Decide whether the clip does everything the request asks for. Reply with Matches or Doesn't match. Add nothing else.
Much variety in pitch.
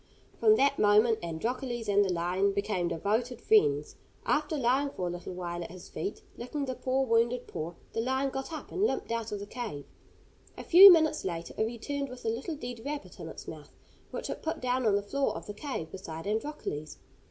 Matches